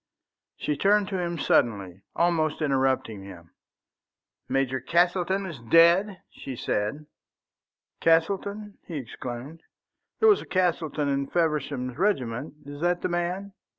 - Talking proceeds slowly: Yes, slow, 120 wpm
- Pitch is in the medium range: Yes, medium, 160 Hz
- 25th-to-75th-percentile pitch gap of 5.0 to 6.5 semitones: Yes, average, 5.3 semitones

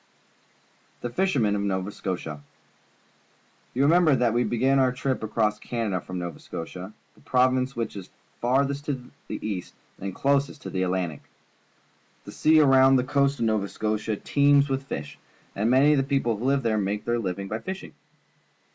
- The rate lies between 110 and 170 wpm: No, average, 180 wpm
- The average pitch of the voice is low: Yes, low, 120 Hz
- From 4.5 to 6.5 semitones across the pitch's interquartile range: Yes, average, 5.1 semitones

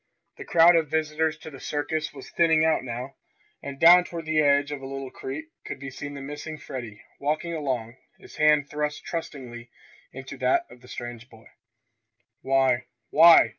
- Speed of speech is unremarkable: Yes, average, 175 wpm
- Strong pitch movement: No, average, 3.1 semitones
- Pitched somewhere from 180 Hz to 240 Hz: No, medium, 145 Hz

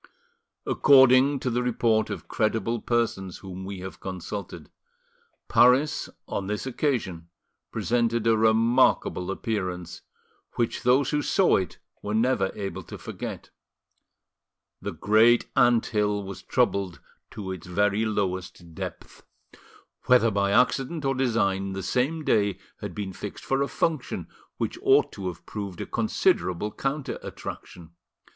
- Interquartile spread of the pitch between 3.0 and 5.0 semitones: Yes, average, 4.5 semitones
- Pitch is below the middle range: Yes, low, 110 Hz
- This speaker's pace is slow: Yes, slow, 130 wpm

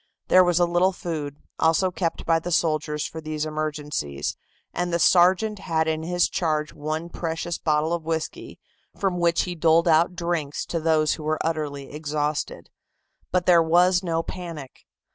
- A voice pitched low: No, medium, 165 Hz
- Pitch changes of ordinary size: No, narrow, 2.2 semitones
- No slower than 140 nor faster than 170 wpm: Yes, average, 165 wpm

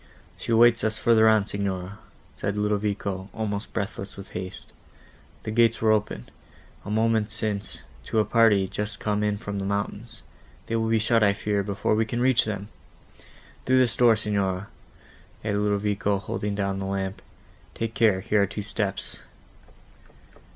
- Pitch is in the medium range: No, low, 105 Hz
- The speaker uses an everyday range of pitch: No, narrow, 1.9 semitones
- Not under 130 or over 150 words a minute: No, average, 160 wpm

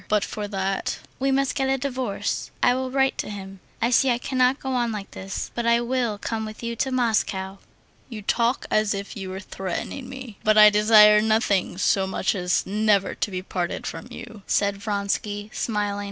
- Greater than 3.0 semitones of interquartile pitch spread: Yes, average, 3.6 semitones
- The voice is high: Yes, high, 215 Hz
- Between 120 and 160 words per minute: No, average, 195 wpm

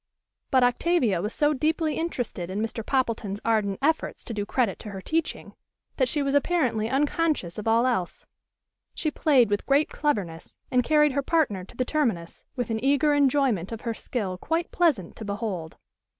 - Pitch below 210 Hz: No, high, 245 Hz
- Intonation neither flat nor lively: No, wide, 6.2 semitones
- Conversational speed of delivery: Yes, average, 180 wpm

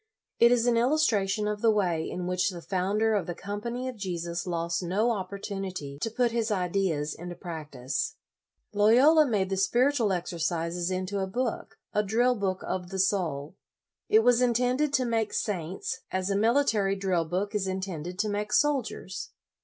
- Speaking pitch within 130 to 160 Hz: No, high, 195 Hz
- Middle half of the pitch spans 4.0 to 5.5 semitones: Yes, average, 4.3 semitones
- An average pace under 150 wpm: No, average, 170 wpm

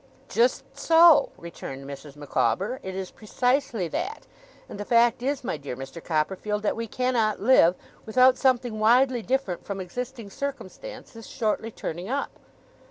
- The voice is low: No, high, 225 Hz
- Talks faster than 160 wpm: No, average, 150 wpm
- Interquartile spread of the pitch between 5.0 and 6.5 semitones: Yes, wide, 5.5 semitones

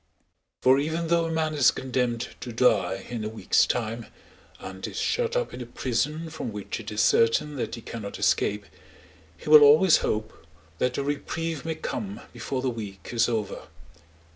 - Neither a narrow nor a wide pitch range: No, wide, 5.8 semitones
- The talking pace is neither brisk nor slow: Yes, average, 180 wpm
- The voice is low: Yes, low, 125 Hz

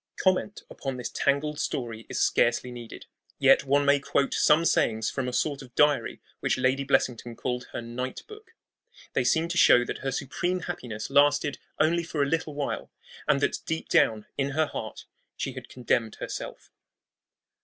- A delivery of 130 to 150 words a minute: No, average, 175 wpm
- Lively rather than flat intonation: No, average, 3.5 semitones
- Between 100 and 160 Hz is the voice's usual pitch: Yes, medium, 140 Hz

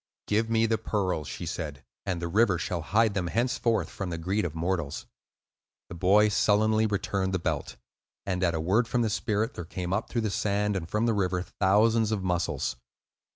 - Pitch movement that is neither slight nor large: Yes, average, 3.6 semitones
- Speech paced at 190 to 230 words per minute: Yes, average, 200 wpm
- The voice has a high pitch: No, low, 100 Hz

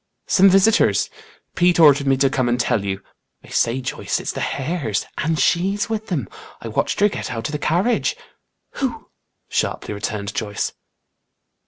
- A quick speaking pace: No, average, 165 wpm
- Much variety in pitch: Yes, wide, 8.0 semitones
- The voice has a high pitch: No, medium, 145 Hz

